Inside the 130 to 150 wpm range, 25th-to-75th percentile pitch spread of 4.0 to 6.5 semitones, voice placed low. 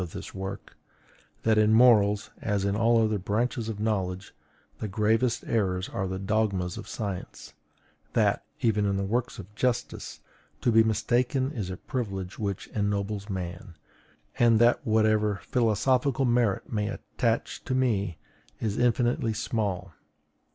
No: average, 140 wpm; average, 2.9 semitones; low, 105 Hz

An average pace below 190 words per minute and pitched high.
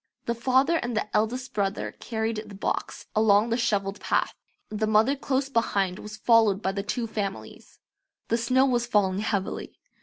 Yes: average, 170 wpm; high, 220 Hz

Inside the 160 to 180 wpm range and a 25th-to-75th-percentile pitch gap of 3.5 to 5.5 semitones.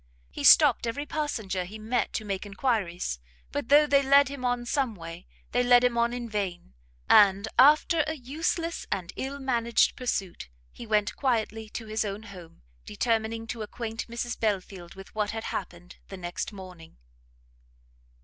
Yes: average, 165 wpm; average, 4.3 semitones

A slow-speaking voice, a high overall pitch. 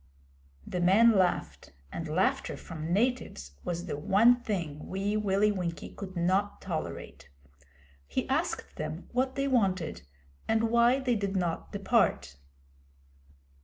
Yes: slow, 130 wpm; high, 195 Hz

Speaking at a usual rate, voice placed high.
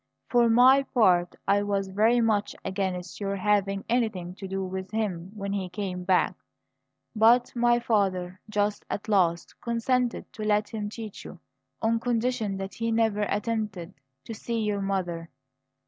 Yes: average, 160 wpm; high, 205 Hz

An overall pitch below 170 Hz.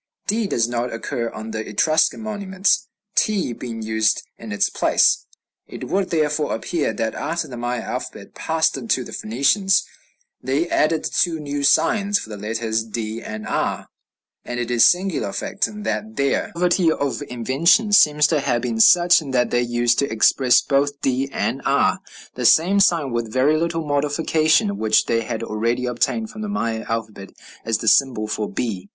Yes: low, 135 Hz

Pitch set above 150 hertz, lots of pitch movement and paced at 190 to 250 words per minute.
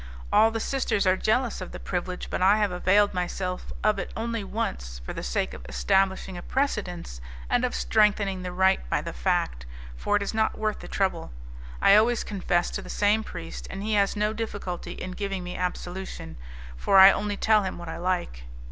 No: high, 190 Hz; average, 2.9 semitones; average, 200 wpm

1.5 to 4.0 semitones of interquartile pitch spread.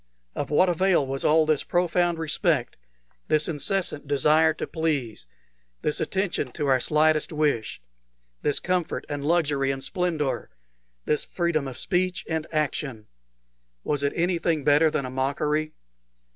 Yes: average, 2.9 semitones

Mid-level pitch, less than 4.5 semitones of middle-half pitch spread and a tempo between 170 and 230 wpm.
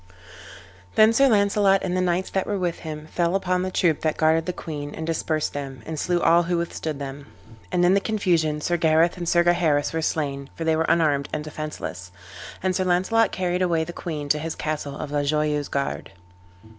Yes: medium, 165 Hz; average, 3.0 semitones; fast, 205 wpm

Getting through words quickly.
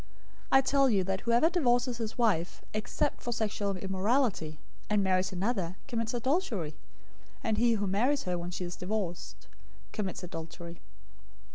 No: average, 150 wpm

